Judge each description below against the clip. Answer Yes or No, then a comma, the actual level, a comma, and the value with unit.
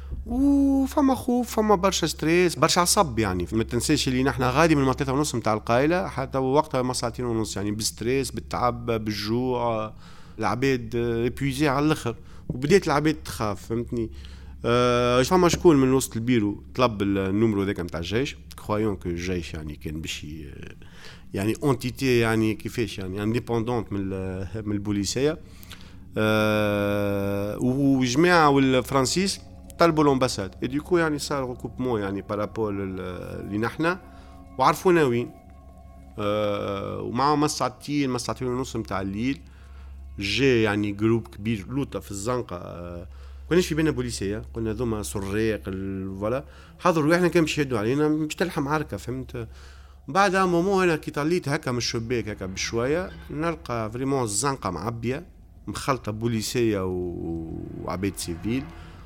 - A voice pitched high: No, low, 115 Hz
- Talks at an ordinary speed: No, slow, 135 wpm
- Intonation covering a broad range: Yes, wide, 5.8 semitones